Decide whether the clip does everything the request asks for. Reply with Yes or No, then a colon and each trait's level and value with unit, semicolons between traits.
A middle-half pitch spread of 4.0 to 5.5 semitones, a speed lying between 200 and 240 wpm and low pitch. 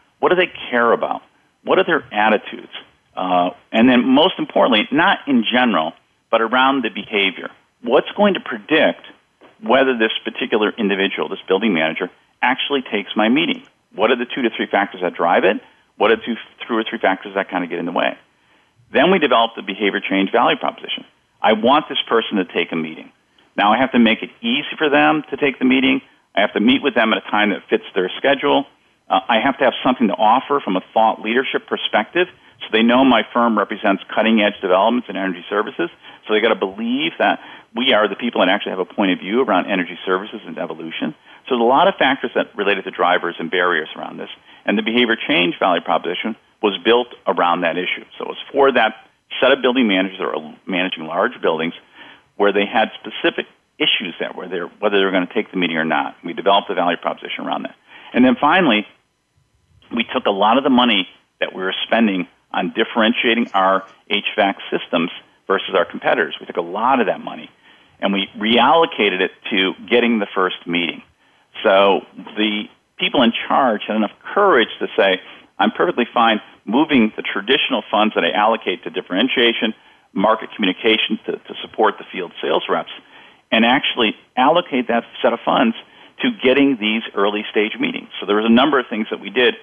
Yes: average, 4.8 semitones; fast, 205 wpm; low, 110 Hz